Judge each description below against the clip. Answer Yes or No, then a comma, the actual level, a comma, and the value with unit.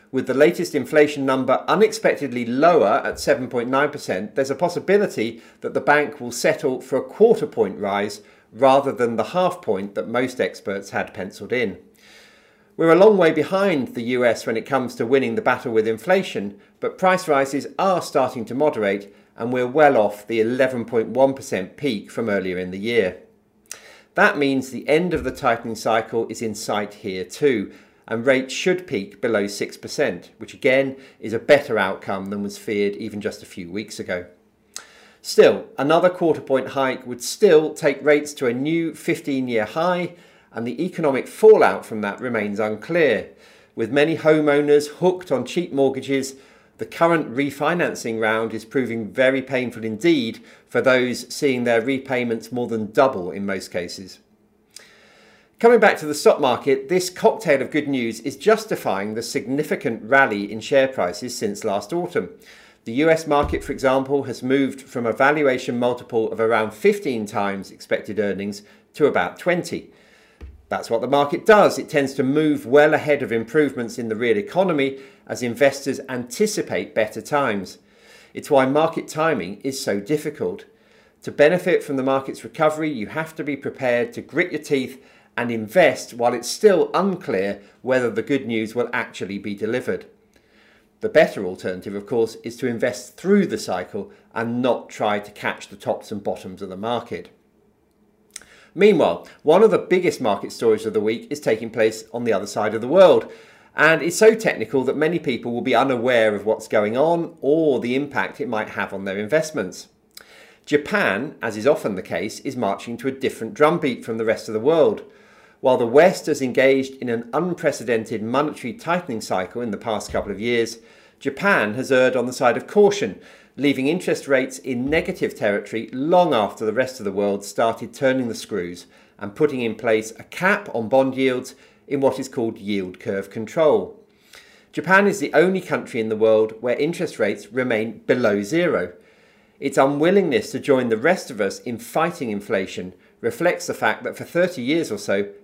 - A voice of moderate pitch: No, low, 130 Hz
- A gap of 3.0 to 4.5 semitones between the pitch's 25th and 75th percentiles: No, average, 5.2 semitones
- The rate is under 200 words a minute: Yes, average, 175 wpm